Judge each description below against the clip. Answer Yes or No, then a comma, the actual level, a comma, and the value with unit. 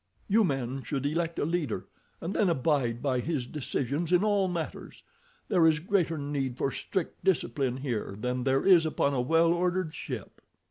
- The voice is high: No, medium, 155 Hz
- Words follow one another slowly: No, average, 175 wpm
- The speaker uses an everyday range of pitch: Yes, average, 4.5 semitones